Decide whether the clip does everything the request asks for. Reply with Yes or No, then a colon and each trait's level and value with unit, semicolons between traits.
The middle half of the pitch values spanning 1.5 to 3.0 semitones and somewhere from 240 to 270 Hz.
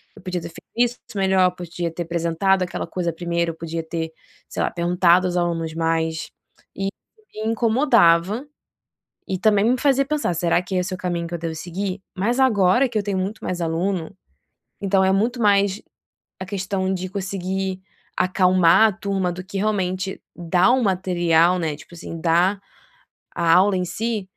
No: average, 2.7 semitones; medium, 185 Hz